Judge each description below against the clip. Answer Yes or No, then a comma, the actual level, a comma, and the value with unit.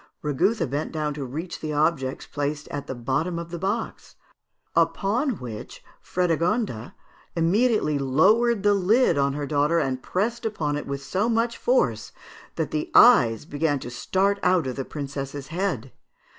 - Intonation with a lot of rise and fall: Yes, wide, 6.3 semitones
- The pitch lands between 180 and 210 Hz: No, medium, 160 Hz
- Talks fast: No, average, 155 wpm